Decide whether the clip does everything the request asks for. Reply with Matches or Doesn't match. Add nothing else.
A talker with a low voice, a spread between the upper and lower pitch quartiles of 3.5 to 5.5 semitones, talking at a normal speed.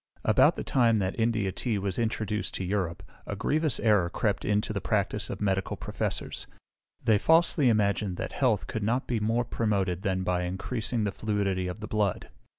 Doesn't match